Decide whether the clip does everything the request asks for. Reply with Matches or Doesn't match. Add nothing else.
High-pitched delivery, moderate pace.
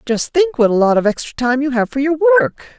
Doesn't match